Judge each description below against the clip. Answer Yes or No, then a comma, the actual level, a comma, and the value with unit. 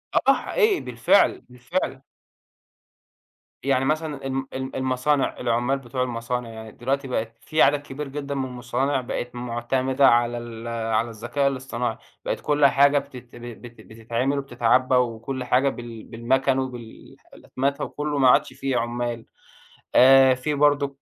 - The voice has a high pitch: No, low, 130 Hz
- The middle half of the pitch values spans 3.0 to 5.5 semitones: No, narrow, 2.5 semitones